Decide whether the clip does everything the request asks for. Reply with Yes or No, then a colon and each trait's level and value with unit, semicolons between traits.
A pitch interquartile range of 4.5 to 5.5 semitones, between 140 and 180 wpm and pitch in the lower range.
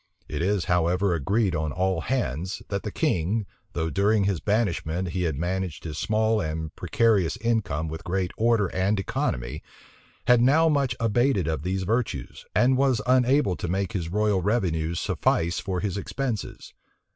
Yes: average, 4.8 semitones; average, 160 wpm; very low, 95 Hz